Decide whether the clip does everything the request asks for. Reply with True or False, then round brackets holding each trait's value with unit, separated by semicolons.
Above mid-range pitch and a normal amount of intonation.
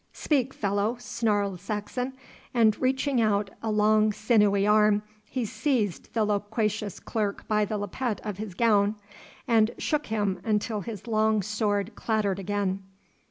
False (215 Hz; 1.7 semitones)